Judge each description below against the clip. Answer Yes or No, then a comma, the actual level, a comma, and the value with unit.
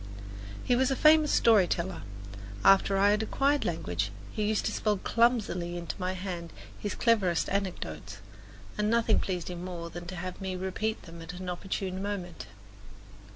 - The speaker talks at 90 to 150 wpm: No, average, 165 wpm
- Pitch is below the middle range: No, high, 190 Hz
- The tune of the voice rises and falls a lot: No, average, 3.4 semitones